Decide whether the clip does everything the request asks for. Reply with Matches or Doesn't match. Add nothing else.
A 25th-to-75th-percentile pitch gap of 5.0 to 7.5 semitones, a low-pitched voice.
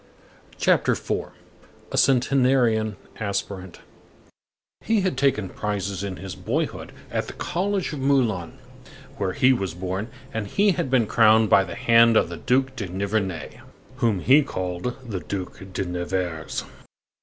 Matches